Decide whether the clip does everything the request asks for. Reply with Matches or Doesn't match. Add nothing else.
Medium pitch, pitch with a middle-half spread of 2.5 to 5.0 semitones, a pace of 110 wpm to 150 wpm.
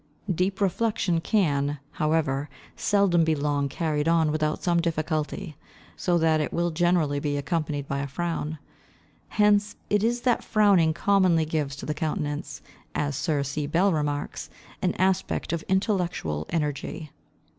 Matches